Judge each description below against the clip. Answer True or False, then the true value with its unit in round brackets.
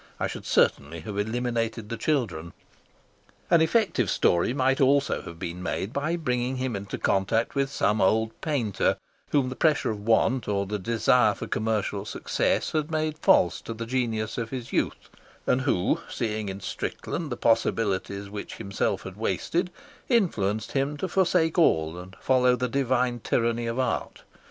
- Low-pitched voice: True (115 Hz)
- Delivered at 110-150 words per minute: False (165 wpm)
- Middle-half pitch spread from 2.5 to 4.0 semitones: False (4.8 semitones)